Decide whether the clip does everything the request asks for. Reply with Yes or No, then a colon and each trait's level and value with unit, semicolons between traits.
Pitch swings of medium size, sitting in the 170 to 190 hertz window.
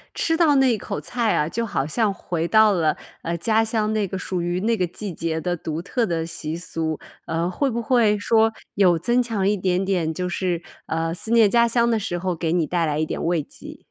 Yes: average, 5.0 semitones; medium, 185 Hz